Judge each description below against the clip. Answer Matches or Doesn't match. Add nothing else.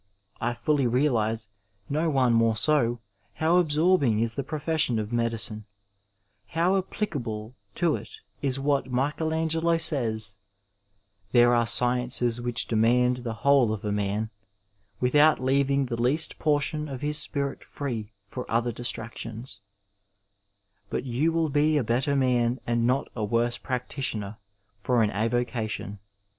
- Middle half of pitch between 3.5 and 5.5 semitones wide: Matches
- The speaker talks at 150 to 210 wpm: Doesn't match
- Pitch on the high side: Doesn't match